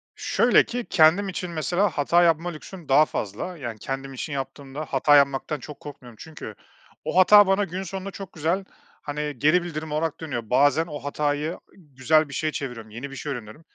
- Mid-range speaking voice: Yes, medium, 150 Hz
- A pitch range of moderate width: Yes, average, 4.0 semitones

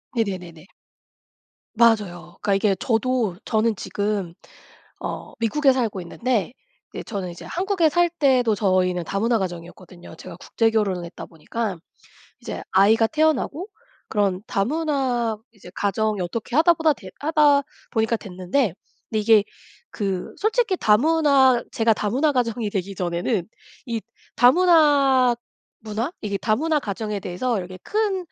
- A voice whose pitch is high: Yes, high, 225 Hz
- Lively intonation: Yes, wide, 5.7 semitones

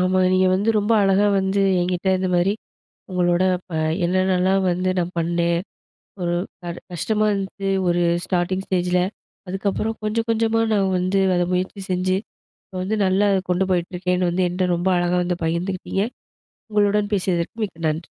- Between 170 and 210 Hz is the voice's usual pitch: Yes, medium, 185 Hz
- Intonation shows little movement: Yes, narrow, 1.7 semitones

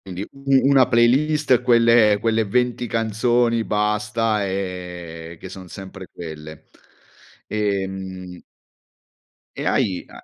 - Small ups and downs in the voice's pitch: No, average, 4.0 semitones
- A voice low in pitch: Yes, low, 105 Hz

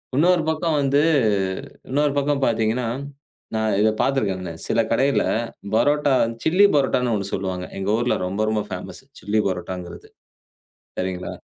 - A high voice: No, low, 115 Hz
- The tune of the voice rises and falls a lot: Yes, wide, 6.4 semitones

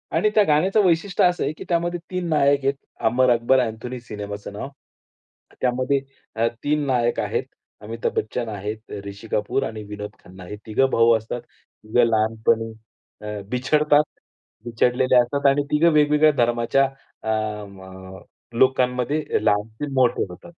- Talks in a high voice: No, low, 125 Hz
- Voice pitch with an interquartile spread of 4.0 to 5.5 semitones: Yes, average, 4.5 semitones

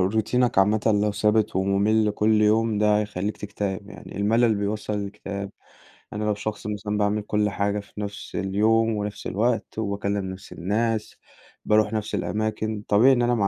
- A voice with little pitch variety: Yes, narrow, 1.2 semitones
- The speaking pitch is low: Yes, low, 105 Hz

